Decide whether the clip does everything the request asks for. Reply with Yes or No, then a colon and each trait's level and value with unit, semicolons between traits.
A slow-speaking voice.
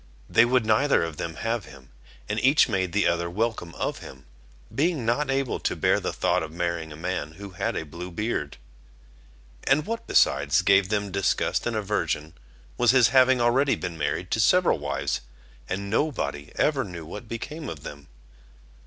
No: average, 180 wpm